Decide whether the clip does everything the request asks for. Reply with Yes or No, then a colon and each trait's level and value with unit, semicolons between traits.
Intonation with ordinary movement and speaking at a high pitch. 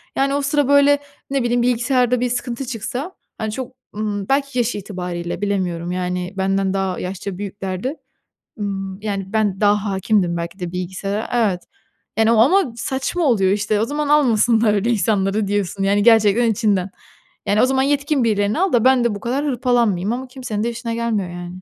Yes: average, 4.3 semitones; high, 215 Hz